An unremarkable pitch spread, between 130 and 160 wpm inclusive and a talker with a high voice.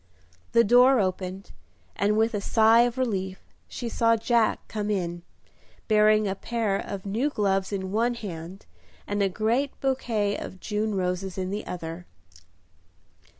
Yes: average, 3.2 semitones; average, 150 wpm; high, 210 Hz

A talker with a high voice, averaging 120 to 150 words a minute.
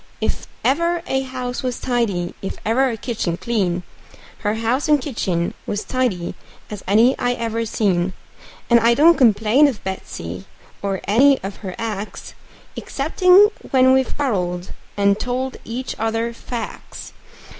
Yes: high, 230 Hz; average, 145 wpm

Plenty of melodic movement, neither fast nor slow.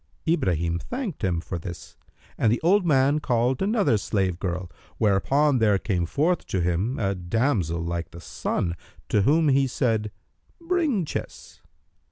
Yes: wide, 8.9 semitones; average, 150 wpm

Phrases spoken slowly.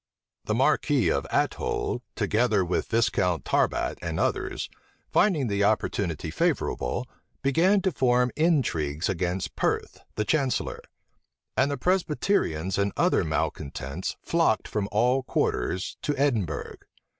Yes: slow, 120 wpm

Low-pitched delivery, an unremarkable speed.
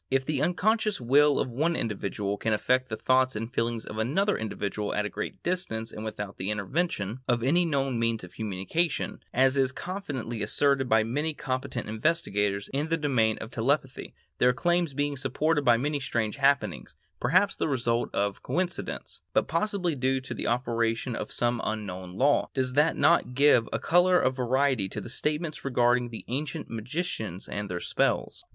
Yes: low, 130 Hz; average, 175 wpm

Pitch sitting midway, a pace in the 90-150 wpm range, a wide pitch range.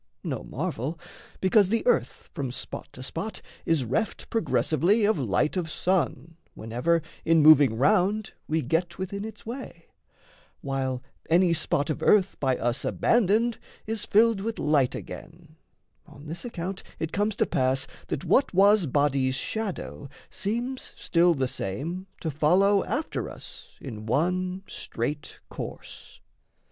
Yes: medium, 170 Hz; average, 140 wpm; wide, 6.3 semitones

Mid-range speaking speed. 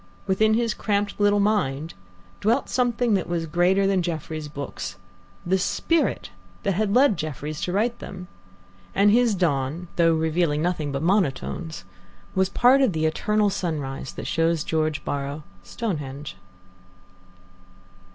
No: slow, 130 wpm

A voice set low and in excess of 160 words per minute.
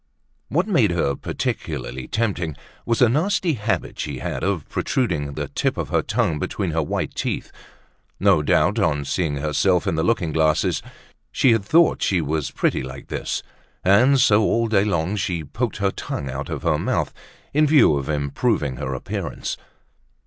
Yes: very low, 90 Hz; average, 170 wpm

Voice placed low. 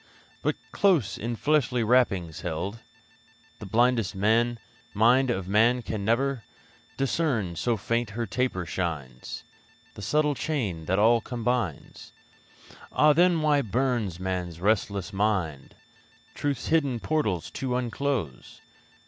Yes: low, 115 Hz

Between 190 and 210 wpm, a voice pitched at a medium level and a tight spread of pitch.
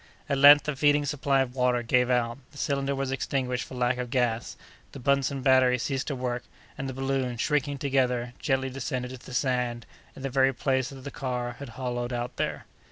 No: fast, 205 wpm; low, 130 Hz; narrow, 1.8 semitones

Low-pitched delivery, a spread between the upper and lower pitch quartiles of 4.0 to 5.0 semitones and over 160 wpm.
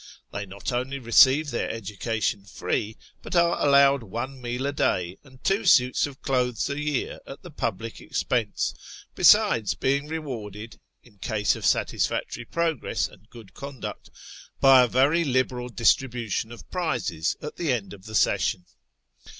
No: low, 125 Hz; average, 4.3 semitones; average, 150 wpm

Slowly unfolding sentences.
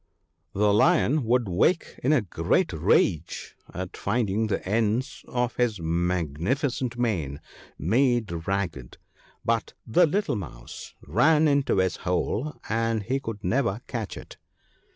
Yes: slow, 130 wpm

